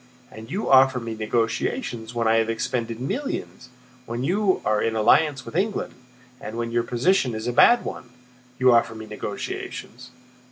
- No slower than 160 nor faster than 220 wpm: Yes, average, 165 wpm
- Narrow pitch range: No, average, 3.1 semitones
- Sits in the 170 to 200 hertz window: No, low, 120 Hz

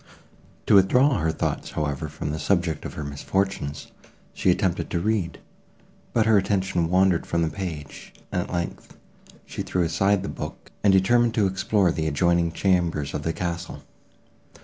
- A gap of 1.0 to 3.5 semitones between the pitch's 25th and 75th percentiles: Yes, average, 3.2 semitones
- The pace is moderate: Yes, average, 165 wpm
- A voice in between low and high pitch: No, very low, 90 Hz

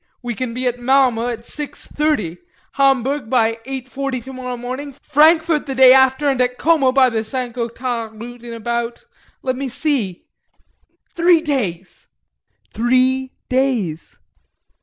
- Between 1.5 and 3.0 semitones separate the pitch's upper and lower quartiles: Yes, narrow, 2.5 semitones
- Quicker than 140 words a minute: No, slow, 135 wpm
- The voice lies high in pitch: Yes, very high, 255 Hz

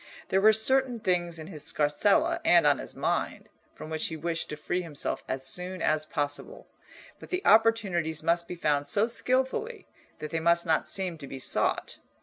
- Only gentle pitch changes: No, wide, 5.4 semitones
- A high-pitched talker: No, medium, 170 Hz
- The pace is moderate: Yes, average, 185 wpm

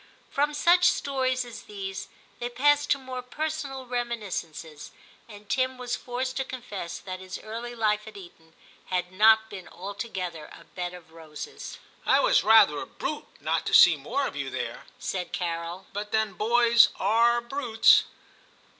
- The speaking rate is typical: Yes, average, 165 wpm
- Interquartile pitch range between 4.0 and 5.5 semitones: Yes, average, 5.2 semitones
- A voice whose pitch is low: No, high, 220 Hz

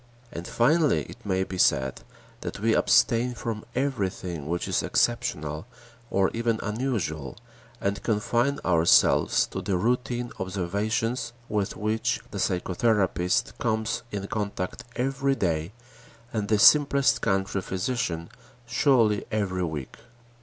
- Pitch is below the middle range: Yes, low, 105 Hz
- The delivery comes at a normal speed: No, slow, 120 wpm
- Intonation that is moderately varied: Yes, average, 4.6 semitones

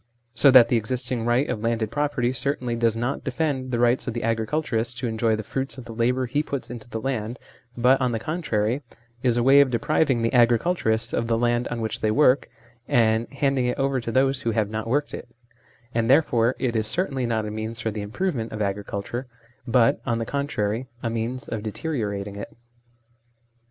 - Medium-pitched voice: No, low, 120 Hz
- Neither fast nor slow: No, fast, 215 wpm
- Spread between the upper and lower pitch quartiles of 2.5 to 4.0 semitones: Yes, average, 2.8 semitones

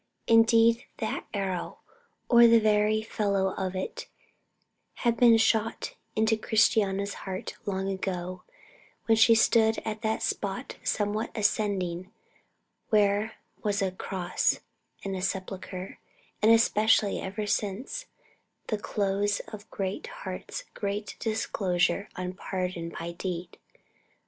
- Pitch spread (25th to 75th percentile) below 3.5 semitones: Yes, narrow, 2.6 semitones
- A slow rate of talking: Yes, slow, 115 wpm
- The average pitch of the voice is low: No, high, 205 Hz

